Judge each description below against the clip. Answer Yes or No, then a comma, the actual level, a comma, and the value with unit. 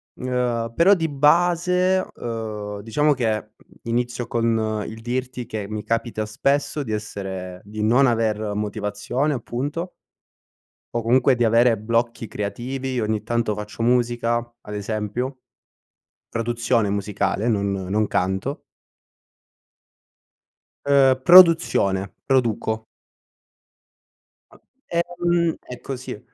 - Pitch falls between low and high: No, low, 115 Hz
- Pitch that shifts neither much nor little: Yes, average, 3.7 semitones